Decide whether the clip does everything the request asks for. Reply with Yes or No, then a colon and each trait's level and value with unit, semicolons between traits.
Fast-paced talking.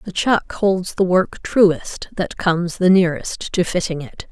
No: average, 180 wpm